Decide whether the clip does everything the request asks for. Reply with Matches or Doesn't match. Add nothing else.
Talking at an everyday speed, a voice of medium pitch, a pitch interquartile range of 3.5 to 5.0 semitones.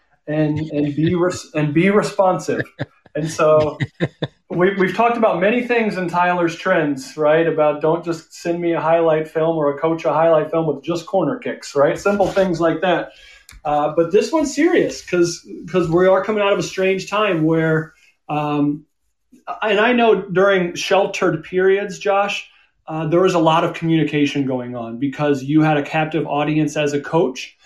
Matches